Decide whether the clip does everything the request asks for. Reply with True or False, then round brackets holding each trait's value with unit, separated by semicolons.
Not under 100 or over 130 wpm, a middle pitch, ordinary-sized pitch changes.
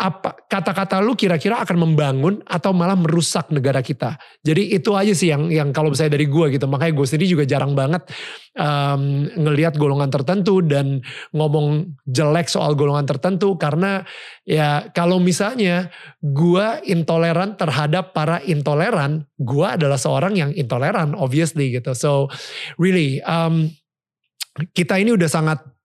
False (140 wpm; 160 Hz; 3.8 semitones)